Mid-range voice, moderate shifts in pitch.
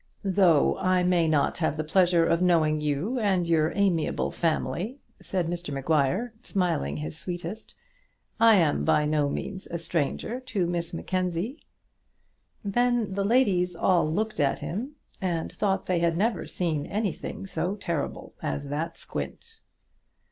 Yes: medium, 175 Hz; average, 3.9 semitones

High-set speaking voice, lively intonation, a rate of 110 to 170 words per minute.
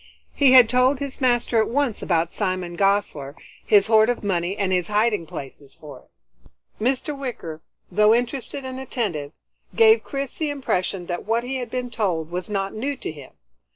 No: high, 215 Hz; wide, 6.1 semitones; average, 180 wpm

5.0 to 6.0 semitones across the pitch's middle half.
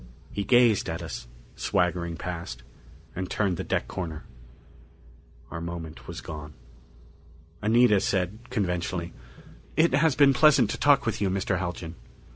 Yes: average, 5.3 semitones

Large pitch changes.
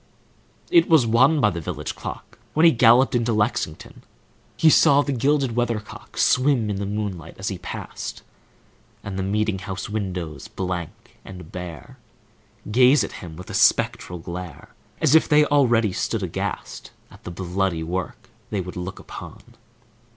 Yes: wide, 5.9 semitones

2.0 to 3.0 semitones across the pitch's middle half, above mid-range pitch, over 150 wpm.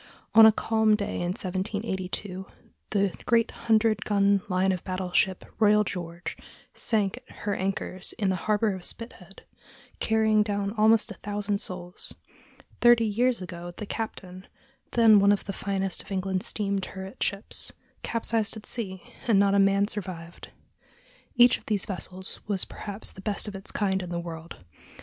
Yes: narrow, 2.4 semitones; high, 200 Hz; average, 165 wpm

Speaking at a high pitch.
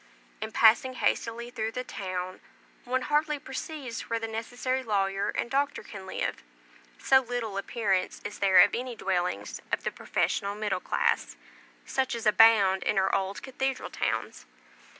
Yes: high, 225 Hz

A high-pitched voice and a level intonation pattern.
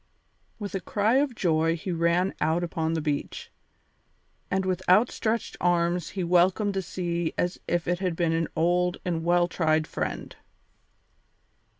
No: medium, 175 Hz; narrow, 2.1 semitones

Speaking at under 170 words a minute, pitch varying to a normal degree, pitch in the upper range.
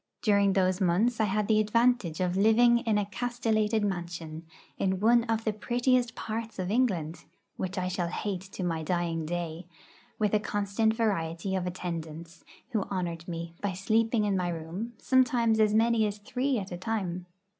No: average, 175 wpm; average, 4.2 semitones; high, 200 Hz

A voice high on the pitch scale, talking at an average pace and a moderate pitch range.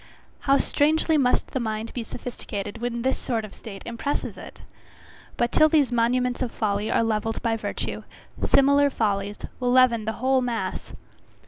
Yes: high, 240 Hz; average, 160 wpm; average, 3.0 semitones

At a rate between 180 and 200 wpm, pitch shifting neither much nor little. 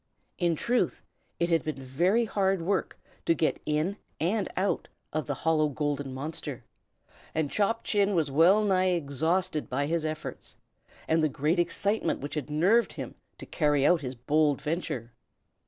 No: average, 160 wpm; average, 4.2 semitones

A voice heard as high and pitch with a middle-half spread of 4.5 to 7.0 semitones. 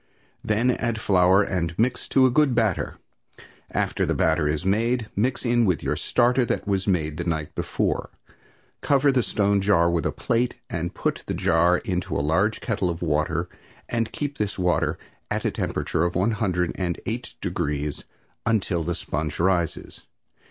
No: very low, 95 Hz; wide, 5.4 semitones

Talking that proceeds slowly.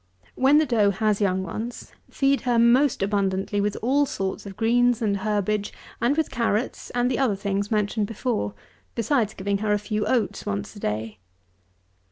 No: average, 180 wpm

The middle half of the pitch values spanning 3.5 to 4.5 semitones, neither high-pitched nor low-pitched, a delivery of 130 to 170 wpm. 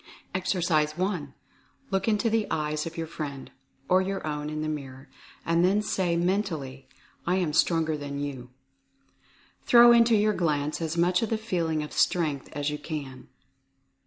Yes: average, 4.0 semitones; medium, 165 Hz; average, 160 wpm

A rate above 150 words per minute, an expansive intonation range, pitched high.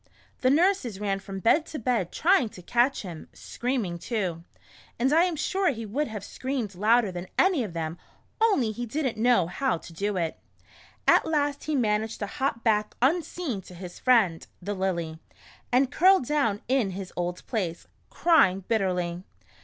Yes: average, 175 wpm; wide, 6.5 semitones; high, 225 Hz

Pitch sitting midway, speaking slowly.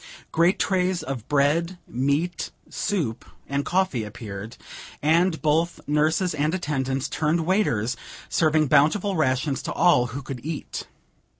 Yes: medium, 150 Hz; slow, 125 wpm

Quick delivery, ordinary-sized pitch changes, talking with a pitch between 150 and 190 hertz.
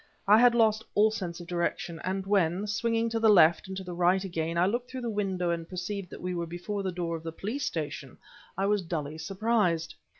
Yes: fast, 230 wpm; average, 3.6 semitones; medium, 185 Hz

